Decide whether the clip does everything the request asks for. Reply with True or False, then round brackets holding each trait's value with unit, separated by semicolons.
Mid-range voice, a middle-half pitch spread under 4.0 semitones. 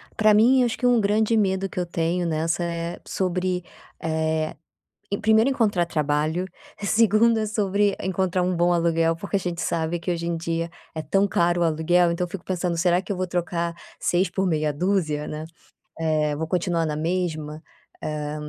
True (175 Hz; 2.9 semitones)